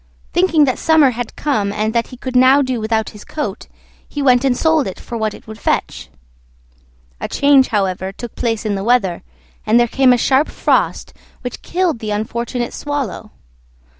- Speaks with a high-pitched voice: Yes, high, 240 Hz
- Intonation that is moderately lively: Yes, average, 4.1 semitones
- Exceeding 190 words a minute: No, average, 185 wpm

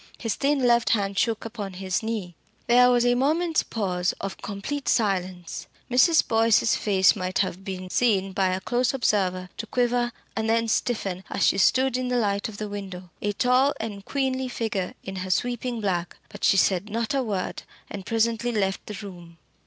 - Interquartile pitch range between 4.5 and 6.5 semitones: No, average, 4.1 semitones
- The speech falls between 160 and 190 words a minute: Yes, average, 185 wpm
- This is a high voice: Yes, high, 215 Hz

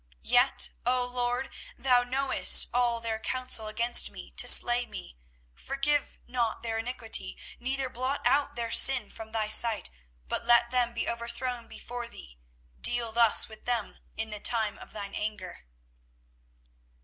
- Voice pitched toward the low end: No, high, 235 Hz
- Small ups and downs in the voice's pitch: Yes, narrow, 2.0 semitones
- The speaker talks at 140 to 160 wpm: Yes, average, 150 wpm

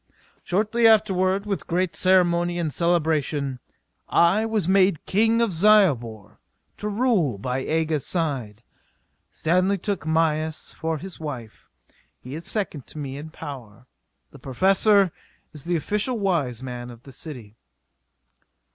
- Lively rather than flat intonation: Yes, wide, 6.1 semitones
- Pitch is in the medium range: Yes, medium, 165 Hz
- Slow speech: Yes, slow, 130 wpm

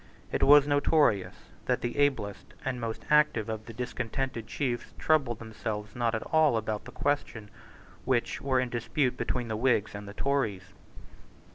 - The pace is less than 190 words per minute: Yes, average, 160 wpm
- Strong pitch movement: No, average, 4.0 semitones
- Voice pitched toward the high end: No, low, 120 Hz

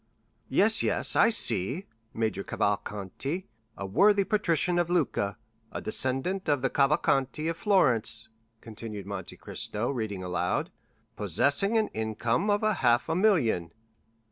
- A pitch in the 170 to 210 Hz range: No, low, 130 Hz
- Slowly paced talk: Yes, slow, 125 wpm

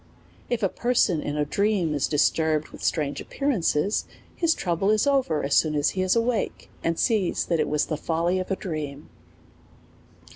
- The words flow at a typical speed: Yes, average, 185 wpm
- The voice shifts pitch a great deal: Yes, wide, 5.8 semitones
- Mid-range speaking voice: Yes, medium, 170 Hz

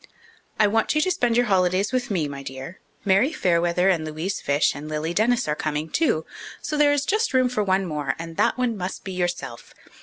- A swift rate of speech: Yes, fast, 215 wpm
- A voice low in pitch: No, medium, 185 Hz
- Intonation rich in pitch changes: Yes, wide, 7.5 semitones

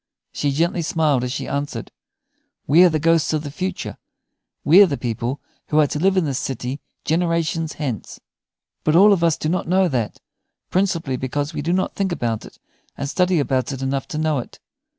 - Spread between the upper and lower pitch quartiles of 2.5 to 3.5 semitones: No, average, 4.0 semitones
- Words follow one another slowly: No, average, 200 wpm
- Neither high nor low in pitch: Yes, medium, 155 Hz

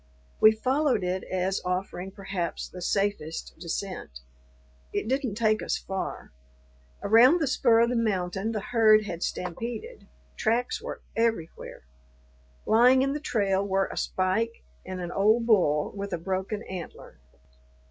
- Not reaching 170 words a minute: Yes, average, 140 wpm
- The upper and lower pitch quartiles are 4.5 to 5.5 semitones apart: No, average, 3.8 semitones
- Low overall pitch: No, high, 200 Hz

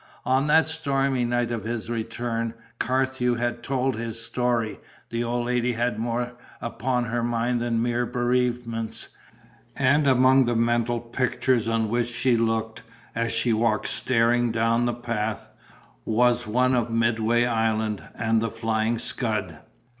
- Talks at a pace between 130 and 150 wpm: Yes, average, 145 wpm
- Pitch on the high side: No, low, 120 Hz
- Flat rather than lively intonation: Yes, narrow, 1.4 semitones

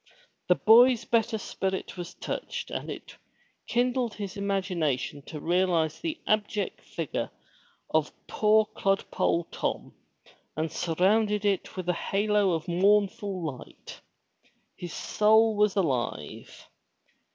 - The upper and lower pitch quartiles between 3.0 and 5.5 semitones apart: Yes, average, 3.7 semitones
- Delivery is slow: Yes, slow, 115 wpm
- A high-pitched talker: Yes, high, 195 Hz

